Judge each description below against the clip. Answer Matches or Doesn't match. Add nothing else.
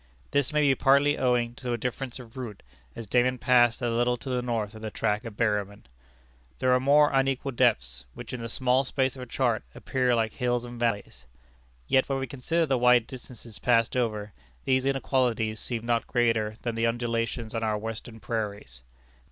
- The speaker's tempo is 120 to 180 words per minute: Doesn't match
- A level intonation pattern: Matches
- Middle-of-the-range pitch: Doesn't match